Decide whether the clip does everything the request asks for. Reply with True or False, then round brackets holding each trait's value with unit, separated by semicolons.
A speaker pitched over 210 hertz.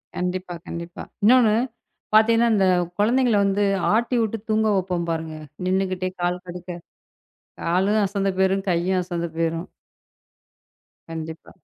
False (185 Hz)